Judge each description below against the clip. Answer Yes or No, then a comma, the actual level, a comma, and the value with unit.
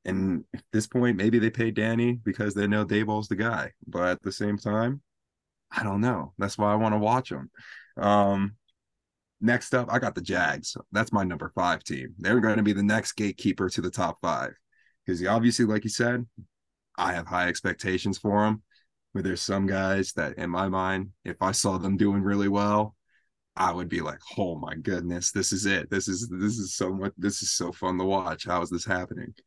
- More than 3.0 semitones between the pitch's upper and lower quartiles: No, narrow, 2.5 semitones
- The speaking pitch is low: Yes, low, 100 Hz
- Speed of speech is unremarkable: No, fast, 210 wpm